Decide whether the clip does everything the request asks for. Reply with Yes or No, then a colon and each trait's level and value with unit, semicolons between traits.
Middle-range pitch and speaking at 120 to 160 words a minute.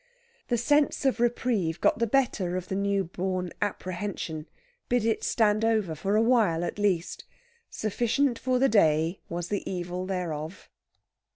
No: high, 200 Hz; average, 155 wpm